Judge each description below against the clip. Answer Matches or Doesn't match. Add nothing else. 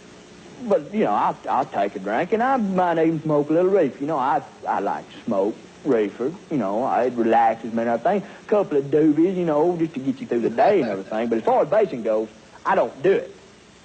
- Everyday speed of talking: Doesn't match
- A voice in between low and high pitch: Matches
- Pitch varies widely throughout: Matches